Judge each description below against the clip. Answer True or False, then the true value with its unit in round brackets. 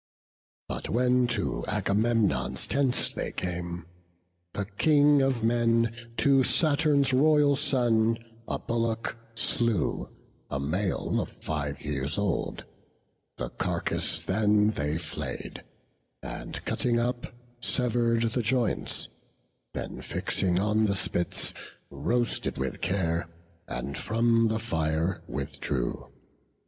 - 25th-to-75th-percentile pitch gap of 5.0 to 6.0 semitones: True (5.4 semitones)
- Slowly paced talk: True (110 wpm)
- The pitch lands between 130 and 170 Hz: False (115 Hz)